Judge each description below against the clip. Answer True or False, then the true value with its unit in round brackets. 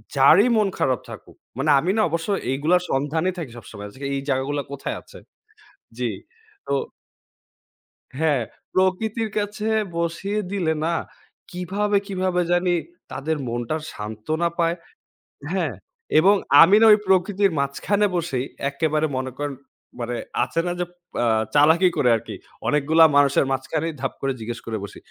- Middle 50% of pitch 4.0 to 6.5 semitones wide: True (5.4 semitones)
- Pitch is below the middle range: False (160 Hz)